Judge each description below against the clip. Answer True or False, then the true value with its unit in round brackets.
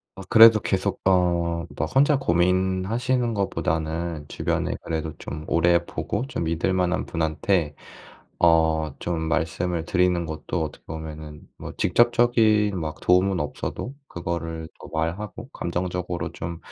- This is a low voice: True (85 Hz)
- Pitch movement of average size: True (3.0 semitones)